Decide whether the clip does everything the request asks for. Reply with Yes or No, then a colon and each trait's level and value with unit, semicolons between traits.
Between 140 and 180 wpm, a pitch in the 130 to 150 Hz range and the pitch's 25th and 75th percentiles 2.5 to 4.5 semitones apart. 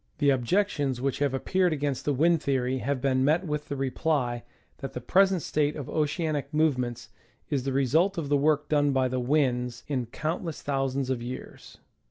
No: average, 190 wpm; medium, 140 Hz; average, 2.9 semitones